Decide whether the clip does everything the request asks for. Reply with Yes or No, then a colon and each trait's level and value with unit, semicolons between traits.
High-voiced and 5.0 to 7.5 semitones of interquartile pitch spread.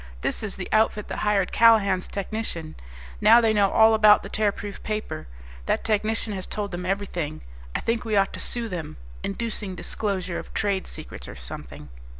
No: high, 200 Hz; average, 3.0 semitones